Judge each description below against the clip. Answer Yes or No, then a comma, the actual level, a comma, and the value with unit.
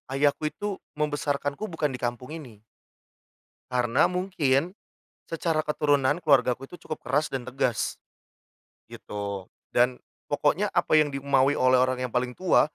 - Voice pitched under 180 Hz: Yes, medium, 140 Hz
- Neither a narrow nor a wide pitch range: Yes, average, 3.2 semitones